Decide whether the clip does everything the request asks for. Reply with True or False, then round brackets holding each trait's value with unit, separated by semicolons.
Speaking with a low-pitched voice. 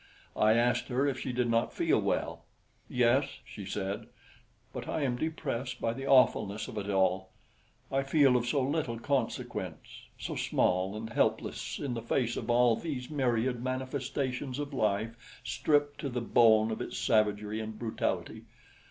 True (120 Hz)